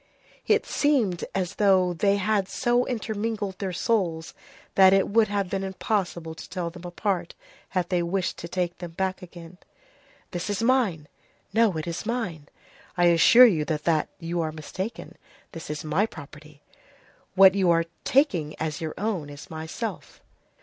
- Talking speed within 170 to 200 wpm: No, average, 155 wpm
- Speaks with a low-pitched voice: No, medium, 185 Hz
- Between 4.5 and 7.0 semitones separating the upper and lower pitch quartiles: No, average, 3.8 semitones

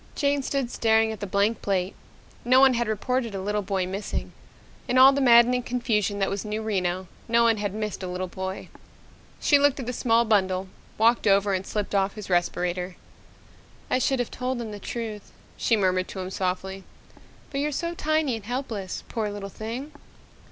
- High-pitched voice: Yes, high, 215 Hz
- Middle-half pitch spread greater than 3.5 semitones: Yes, average, 4.2 semitones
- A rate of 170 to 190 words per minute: Yes, average, 185 wpm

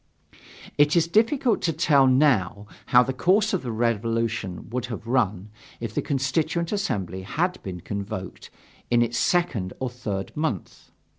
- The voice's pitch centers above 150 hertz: No, low, 125 Hz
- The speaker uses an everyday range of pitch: No, wide, 7.2 semitones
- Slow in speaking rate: No, average, 150 wpm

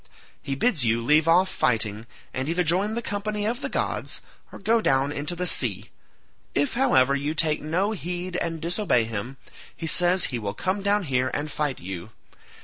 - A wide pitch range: Yes, wide, 6.4 semitones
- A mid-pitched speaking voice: Yes, medium, 160 Hz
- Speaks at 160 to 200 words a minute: Yes, average, 185 wpm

